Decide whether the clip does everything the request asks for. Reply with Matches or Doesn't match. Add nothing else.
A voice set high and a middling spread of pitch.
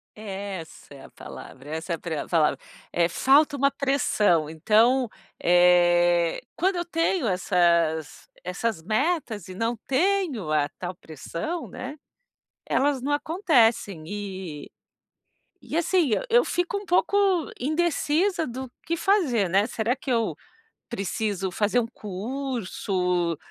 Doesn't match